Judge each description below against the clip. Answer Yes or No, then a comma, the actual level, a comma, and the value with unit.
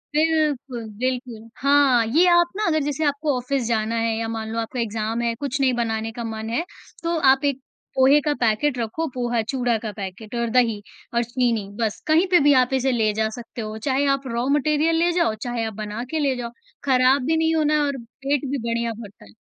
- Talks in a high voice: Yes, high, 245 Hz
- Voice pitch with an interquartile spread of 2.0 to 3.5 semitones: No, average, 4.1 semitones